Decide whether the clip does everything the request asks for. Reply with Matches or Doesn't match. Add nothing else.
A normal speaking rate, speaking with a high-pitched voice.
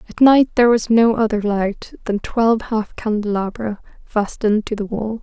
Matches